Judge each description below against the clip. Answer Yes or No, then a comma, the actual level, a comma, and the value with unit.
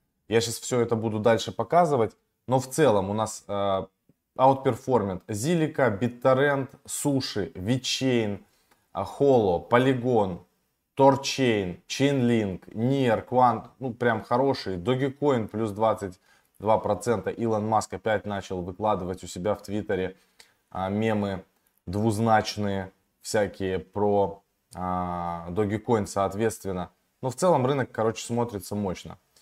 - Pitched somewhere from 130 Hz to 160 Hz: No, low, 110 Hz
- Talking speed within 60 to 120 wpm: Yes, slow, 110 wpm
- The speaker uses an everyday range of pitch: Yes, average, 4.2 semitones